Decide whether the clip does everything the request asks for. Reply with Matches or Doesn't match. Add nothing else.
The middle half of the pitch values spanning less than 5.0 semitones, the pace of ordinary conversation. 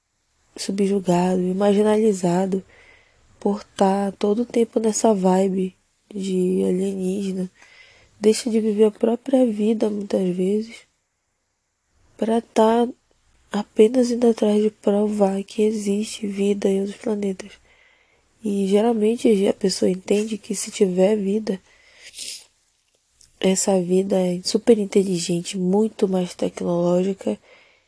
Doesn't match